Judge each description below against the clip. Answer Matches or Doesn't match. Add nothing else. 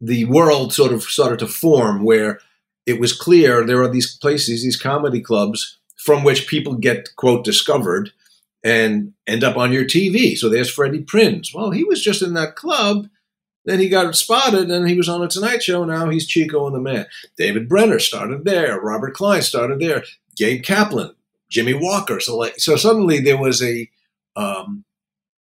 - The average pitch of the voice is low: Doesn't match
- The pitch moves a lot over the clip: Matches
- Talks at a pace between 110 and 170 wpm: Doesn't match